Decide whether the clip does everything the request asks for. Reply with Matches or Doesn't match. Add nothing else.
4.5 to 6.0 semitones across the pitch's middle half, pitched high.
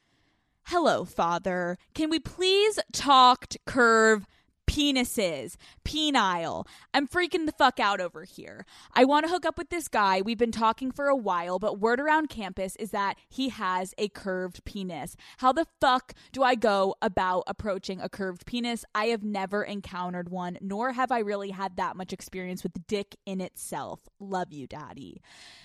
Matches